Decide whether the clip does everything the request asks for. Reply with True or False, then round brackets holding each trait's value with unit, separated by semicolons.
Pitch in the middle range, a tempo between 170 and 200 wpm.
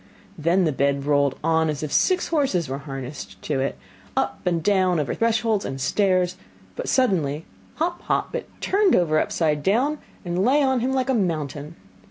True (175 Hz; 180 wpm)